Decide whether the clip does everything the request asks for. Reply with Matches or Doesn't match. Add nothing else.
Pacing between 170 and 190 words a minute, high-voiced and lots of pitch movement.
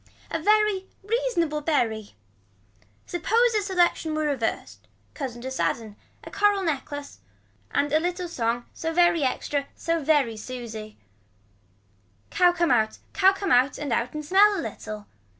Doesn't match